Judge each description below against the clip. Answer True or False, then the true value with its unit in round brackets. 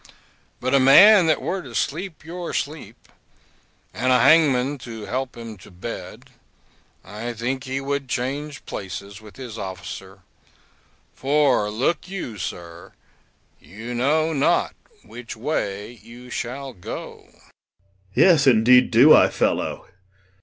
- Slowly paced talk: True (130 wpm)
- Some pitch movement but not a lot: True (4.5 semitones)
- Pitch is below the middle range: True (125 Hz)